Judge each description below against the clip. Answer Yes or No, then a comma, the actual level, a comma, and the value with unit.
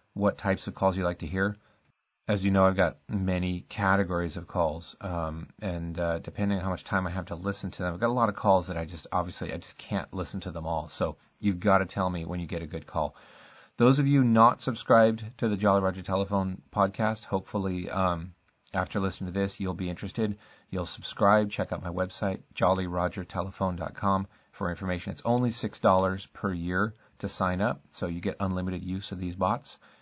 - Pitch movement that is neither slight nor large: No, narrow, 2.1 semitones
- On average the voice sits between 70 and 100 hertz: Yes, very low, 95 Hz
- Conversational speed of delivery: No, fast, 210 wpm